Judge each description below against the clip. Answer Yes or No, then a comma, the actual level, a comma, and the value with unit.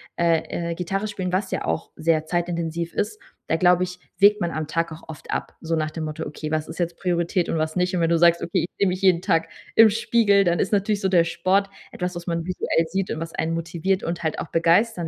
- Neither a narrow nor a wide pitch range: No, narrow, 2.3 semitones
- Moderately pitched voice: Yes, medium, 170 Hz